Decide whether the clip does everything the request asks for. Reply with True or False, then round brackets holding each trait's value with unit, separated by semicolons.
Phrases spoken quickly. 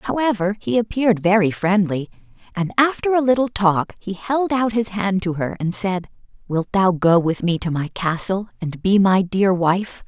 False (190 wpm)